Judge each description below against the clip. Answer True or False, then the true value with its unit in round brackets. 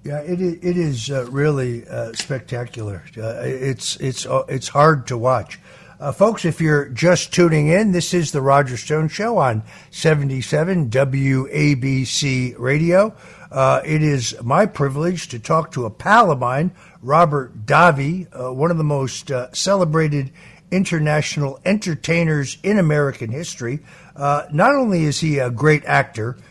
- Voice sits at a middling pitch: True (145 Hz)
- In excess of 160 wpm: False (150 wpm)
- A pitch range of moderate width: True (4.3 semitones)